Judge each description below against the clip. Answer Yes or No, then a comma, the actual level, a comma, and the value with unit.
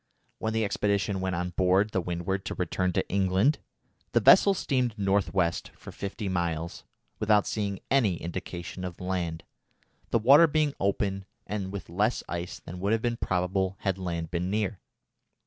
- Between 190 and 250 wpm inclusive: No, average, 165 wpm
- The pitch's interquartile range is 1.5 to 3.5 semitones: Yes, average, 2.8 semitones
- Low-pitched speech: Yes, very low, 95 Hz